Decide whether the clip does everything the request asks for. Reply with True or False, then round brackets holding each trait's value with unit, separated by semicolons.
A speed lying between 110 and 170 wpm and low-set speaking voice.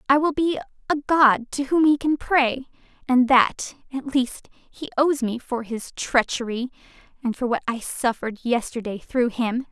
False (165 wpm; 255 Hz)